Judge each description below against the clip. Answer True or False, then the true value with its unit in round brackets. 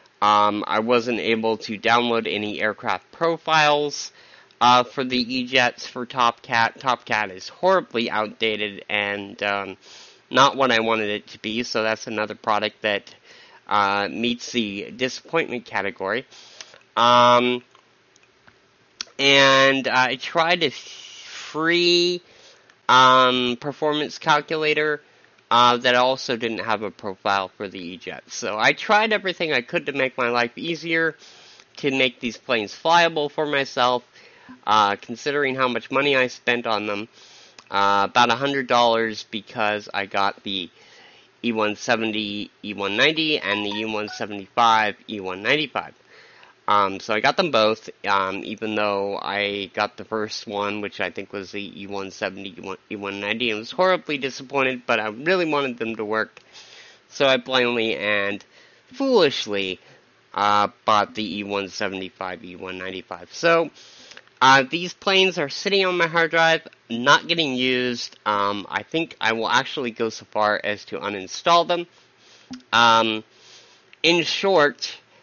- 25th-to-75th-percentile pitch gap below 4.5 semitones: False (4.9 semitones)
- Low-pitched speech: True (120 Hz)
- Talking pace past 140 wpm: False (135 wpm)